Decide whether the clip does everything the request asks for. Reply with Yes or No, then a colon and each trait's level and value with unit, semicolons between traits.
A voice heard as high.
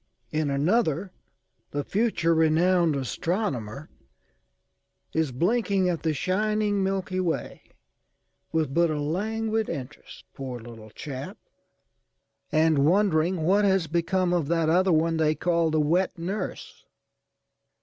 No: medium, 165 Hz